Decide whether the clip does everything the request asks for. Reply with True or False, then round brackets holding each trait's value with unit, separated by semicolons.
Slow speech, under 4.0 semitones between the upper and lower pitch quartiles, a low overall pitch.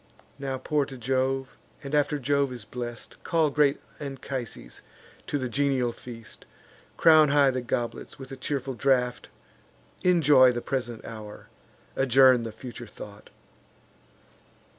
True (130 wpm; 2.5 semitones; 130 Hz)